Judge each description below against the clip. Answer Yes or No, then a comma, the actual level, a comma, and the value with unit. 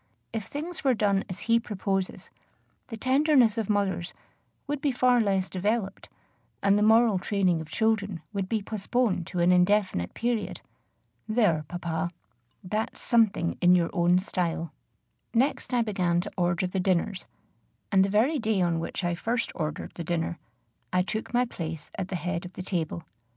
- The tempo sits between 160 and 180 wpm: Yes, average, 165 wpm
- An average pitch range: Yes, average, 4.1 semitones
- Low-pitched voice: No, high, 195 Hz